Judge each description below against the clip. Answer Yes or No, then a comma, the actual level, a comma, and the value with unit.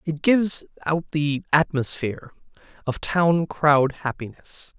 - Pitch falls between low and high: Yes, medium, 150 Hz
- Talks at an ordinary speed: No, slow, 115 wpm